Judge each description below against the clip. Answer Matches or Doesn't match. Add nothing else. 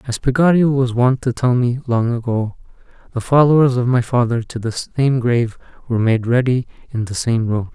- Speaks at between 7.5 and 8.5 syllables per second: Doesn't match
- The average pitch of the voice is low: Matches